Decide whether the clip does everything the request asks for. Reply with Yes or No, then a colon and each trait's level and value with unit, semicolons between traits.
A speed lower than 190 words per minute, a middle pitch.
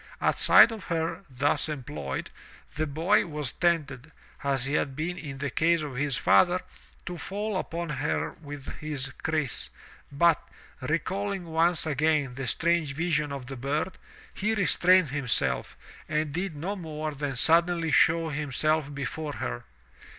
Yes: average, 150 wpm; medium, 155 Hz